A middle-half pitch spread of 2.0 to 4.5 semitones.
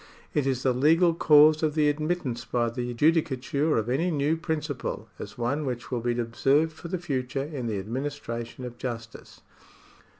Yes: average, 4.2 semitones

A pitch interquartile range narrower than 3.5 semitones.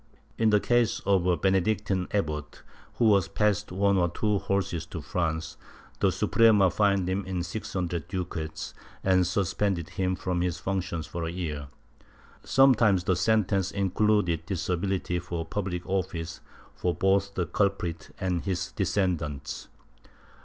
Yes: narrow, 2.5 semitones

